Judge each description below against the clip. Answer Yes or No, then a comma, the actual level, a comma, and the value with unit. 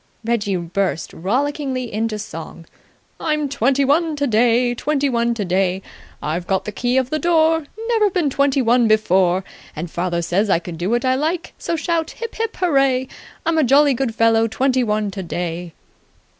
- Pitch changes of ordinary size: No, wide, 6.7 semitones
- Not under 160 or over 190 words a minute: Yes, average, 170 wpm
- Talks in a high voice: Yes, high, 240 Hz